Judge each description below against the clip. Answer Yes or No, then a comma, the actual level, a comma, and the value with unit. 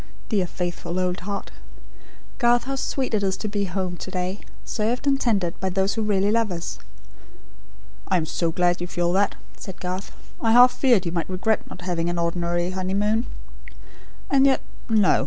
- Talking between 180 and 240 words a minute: Yes, average, 185 wpm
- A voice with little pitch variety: No, average, 3.7 semitones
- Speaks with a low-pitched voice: No, high, 190 Hz